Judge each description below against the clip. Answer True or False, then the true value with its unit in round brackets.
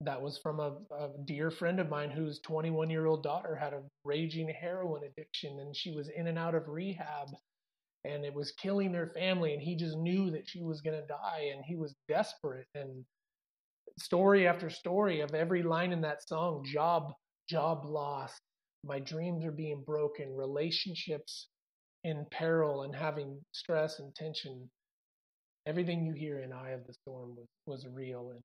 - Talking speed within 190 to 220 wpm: False (180 wpm)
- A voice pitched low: False (155 Hz)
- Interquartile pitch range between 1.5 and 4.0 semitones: True (2.5 semitones)